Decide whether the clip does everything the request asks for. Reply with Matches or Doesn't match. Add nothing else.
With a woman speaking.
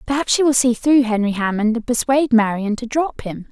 Matches